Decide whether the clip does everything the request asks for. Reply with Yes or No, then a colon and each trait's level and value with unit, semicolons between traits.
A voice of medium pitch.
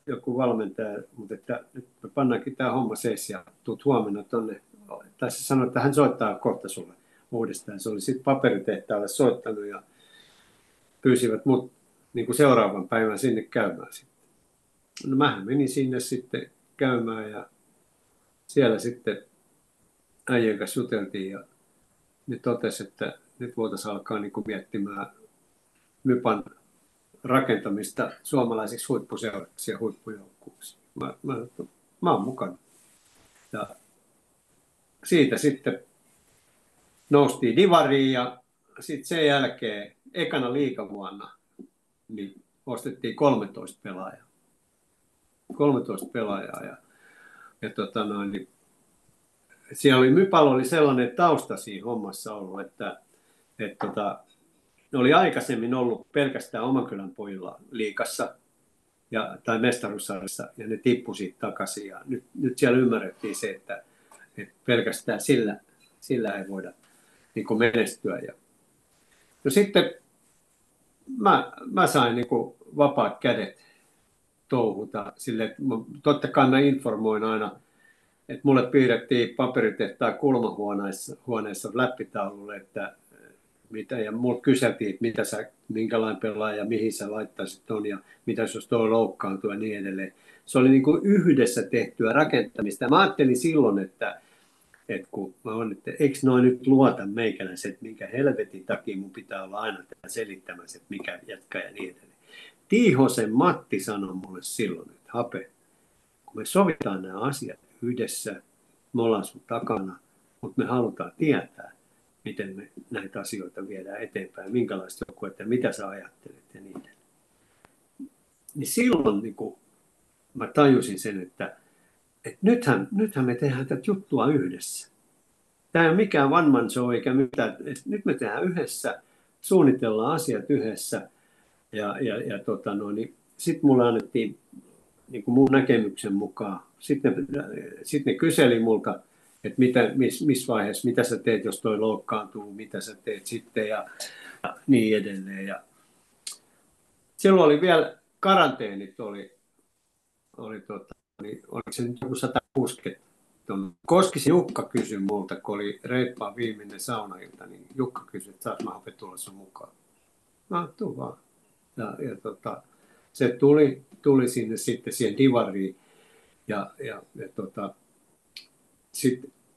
No: low, 120 Hz